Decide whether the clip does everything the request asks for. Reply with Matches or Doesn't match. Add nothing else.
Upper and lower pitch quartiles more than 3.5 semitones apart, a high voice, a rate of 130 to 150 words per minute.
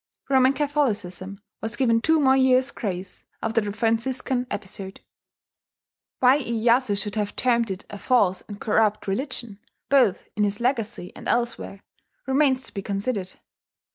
Matches